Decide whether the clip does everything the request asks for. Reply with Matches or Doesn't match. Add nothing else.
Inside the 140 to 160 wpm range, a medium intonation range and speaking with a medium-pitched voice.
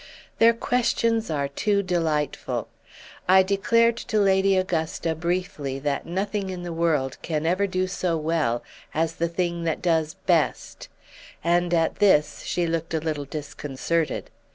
Matches